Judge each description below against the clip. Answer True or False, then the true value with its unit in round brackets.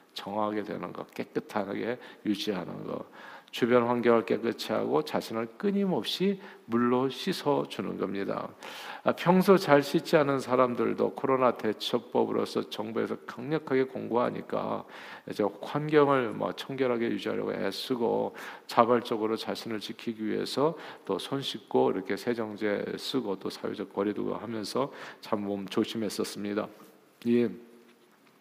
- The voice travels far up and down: False (4.0 semitones)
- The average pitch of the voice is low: True (120 Hz)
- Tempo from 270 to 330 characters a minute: True (295 characters per minute)